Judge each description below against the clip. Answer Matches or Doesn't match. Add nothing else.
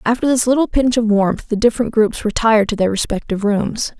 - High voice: Matches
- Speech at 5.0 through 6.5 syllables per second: Matches